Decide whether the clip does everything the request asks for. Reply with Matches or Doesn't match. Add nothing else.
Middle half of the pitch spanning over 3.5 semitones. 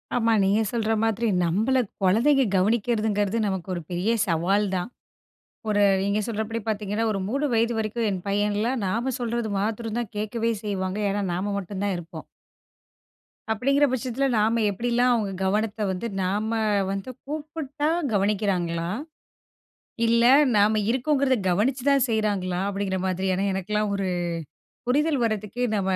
Doesn't match